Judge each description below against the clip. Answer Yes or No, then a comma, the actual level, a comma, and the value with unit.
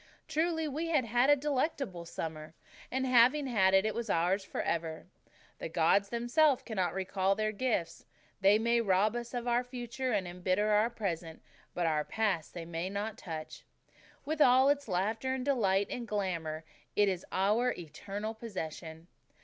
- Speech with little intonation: No, wide, 5.6 semitones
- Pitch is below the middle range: No, high, 210 Hz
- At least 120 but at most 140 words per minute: No, average, 165 wpm